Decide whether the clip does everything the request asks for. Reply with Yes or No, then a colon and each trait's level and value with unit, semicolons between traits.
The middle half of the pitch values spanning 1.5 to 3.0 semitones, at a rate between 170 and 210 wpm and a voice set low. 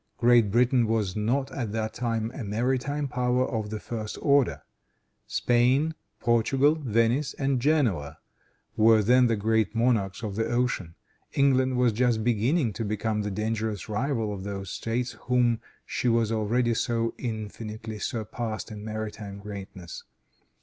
No: average, 2.7 semitones; average, 145 wpm; low, 115 Hz